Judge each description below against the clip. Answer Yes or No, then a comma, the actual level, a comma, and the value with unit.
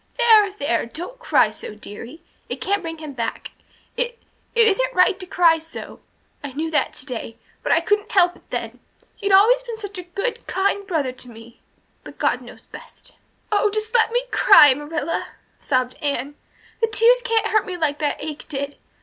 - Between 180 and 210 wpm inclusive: Yes, average, 185 wpm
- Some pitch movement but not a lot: No, wide, 7.1 semitones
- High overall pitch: Yes, very high, 360 Hz